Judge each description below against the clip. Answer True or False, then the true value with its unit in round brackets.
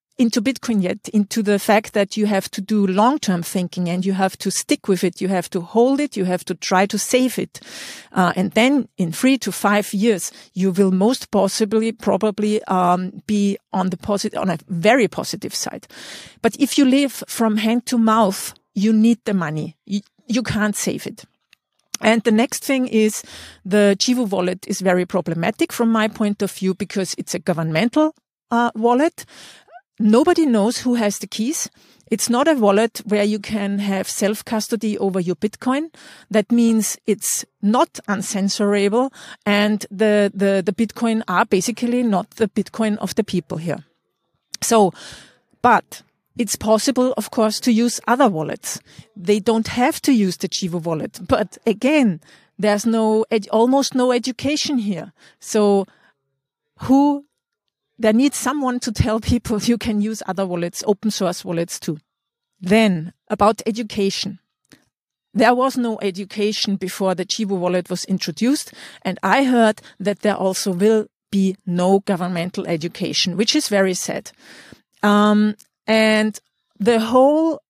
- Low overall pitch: False (210 Hz)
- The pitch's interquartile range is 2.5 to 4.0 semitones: True (3.3 semitones)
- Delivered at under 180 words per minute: True (160 wpm)